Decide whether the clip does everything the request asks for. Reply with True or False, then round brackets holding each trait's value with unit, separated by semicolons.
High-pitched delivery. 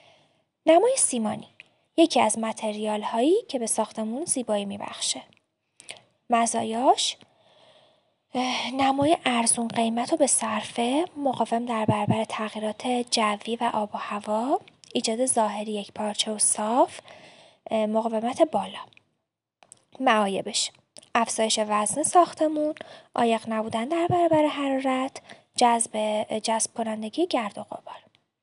True (235 Hz)